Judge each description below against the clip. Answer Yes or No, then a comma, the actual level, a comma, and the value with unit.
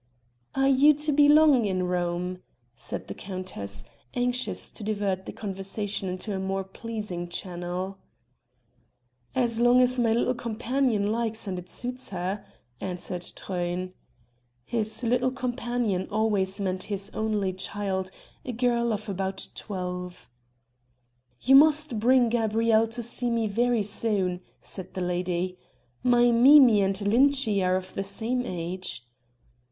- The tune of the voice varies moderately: Yes, average, 4.5 semitones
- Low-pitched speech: No, high, 210 Hz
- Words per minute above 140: No, slow, 135 wpm